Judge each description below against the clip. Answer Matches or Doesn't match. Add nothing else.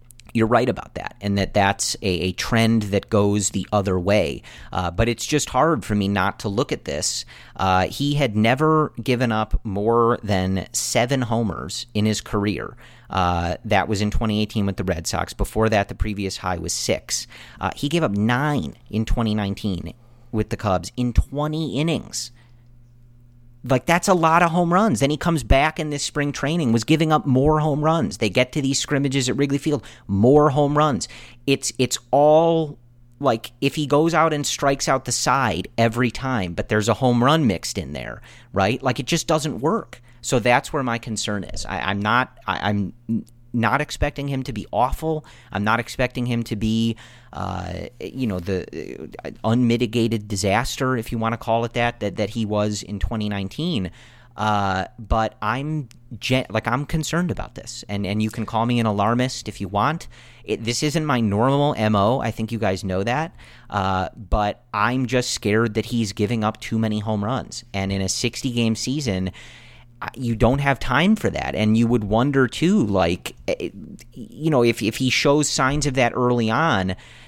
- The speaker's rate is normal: Matches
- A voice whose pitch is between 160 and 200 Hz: Doesn't match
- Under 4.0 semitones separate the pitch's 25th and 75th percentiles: Doesn't match